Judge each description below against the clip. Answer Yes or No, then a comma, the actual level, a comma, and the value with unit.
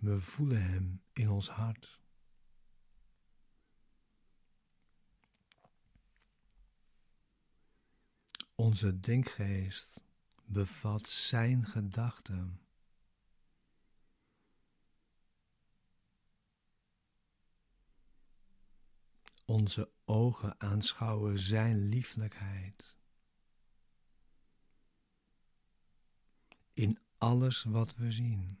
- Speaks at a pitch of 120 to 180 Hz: No, low, 110 Hz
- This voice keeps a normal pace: No, slow, 45 wpm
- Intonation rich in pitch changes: No, narrow, 2.4 semitones